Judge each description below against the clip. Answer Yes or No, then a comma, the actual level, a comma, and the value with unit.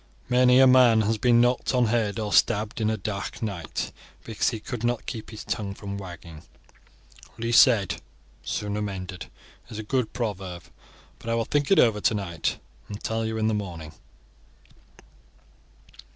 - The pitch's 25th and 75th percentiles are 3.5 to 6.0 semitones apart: No, average, 2.9 semitones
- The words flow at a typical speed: Yes, average, 165 wpm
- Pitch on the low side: Yes, low, 110 Hz